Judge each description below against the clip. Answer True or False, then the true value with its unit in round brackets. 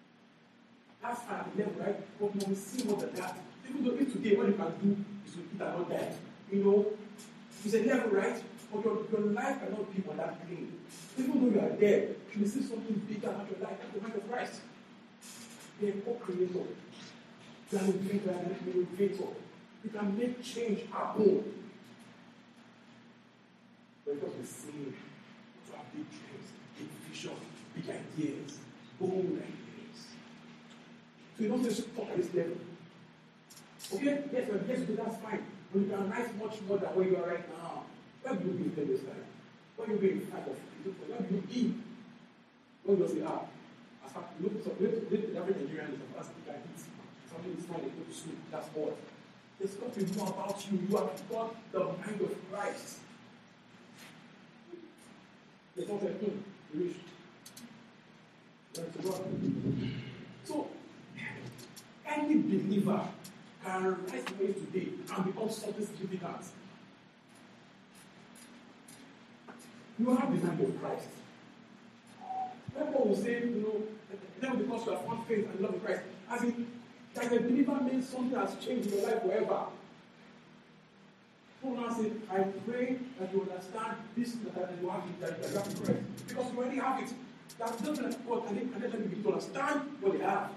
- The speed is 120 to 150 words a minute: False (165 wpm)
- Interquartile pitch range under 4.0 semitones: True (3.2 semitones)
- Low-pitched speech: False (215 Hz)